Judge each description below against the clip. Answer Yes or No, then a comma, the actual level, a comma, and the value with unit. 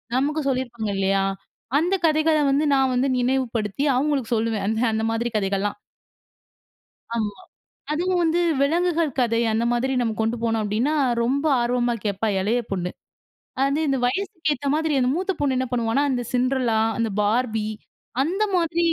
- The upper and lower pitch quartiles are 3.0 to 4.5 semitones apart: No, average, 5.1 semitones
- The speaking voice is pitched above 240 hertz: Yes, very high, 250 Hz